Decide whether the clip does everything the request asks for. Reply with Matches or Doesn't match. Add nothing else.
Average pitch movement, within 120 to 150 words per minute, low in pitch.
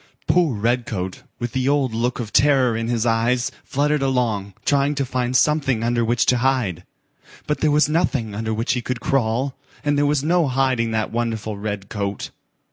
Doesn't match